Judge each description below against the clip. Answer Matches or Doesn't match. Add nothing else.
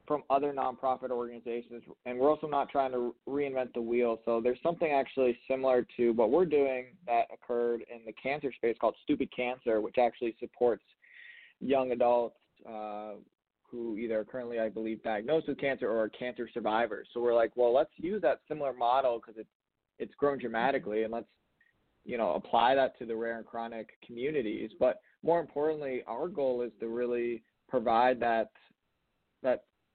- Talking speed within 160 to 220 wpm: Matches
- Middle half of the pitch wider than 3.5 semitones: Doesn't match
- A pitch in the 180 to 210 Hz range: Doesn't match